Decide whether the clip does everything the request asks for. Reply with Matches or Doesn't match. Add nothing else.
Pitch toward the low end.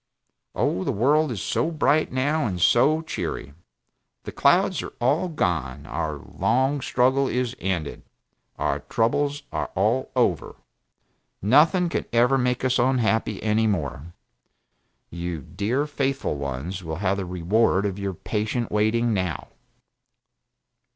Matches